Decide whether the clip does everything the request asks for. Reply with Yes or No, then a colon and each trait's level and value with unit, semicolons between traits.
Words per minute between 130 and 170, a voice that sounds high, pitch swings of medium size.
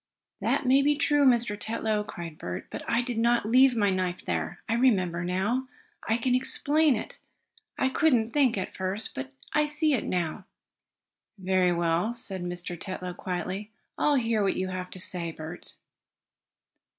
No: average, 165 wpm; high, 210 Hz; wide, 5.8 semitones